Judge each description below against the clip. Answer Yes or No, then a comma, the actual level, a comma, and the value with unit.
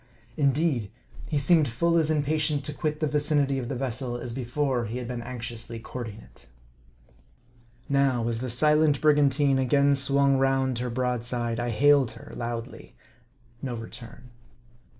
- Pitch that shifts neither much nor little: Yes, average, 3.4 semitones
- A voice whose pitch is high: No, low, 130 Hz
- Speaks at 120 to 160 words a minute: Yes, average, 150 wpm